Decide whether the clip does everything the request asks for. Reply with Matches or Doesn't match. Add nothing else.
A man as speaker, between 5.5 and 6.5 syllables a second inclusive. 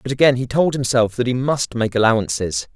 Matches